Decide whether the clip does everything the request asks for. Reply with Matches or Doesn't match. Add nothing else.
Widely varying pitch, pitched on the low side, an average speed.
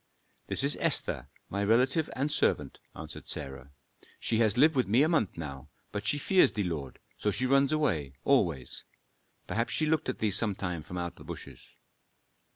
Matches